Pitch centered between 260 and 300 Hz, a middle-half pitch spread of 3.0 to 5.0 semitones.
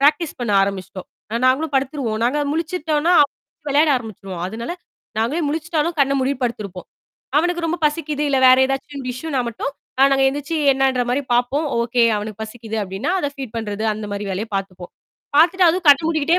No: very high, 270 Hz; wide, 5.6 semitones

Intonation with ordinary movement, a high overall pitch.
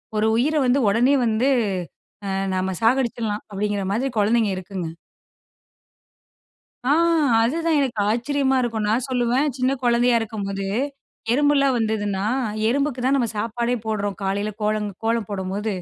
Yes: average, 3.8 semitones; high, 230 Hz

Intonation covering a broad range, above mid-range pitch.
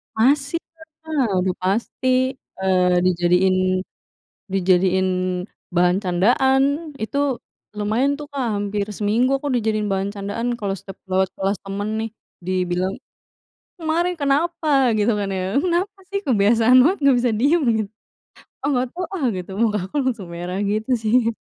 Yes: wide, 6.1 semitones; high, 215 Hz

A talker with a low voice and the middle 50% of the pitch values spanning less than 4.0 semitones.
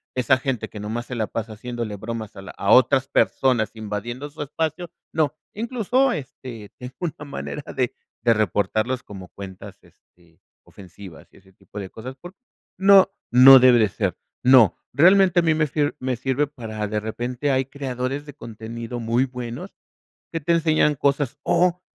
No: low, 125 Hz; average, 4.8 semitones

